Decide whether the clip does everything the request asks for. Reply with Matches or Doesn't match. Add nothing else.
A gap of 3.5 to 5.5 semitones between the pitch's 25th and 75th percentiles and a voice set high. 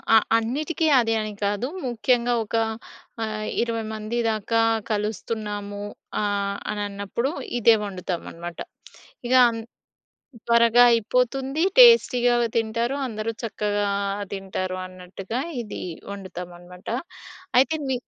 Doesn't match